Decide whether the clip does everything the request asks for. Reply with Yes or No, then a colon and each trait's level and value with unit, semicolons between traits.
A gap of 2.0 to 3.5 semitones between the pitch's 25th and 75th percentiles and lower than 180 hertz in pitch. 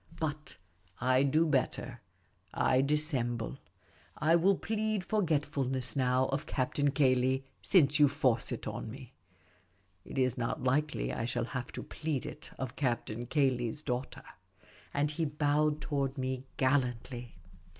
Yes: average, 3.0 semitones; low, 135 Hz